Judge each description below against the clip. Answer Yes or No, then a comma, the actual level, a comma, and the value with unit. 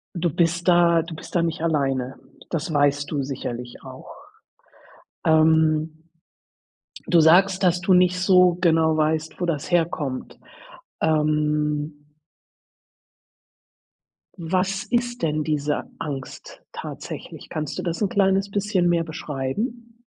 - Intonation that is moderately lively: Yes, average, 3.1 semitones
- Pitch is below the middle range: No, medium, 160 Hz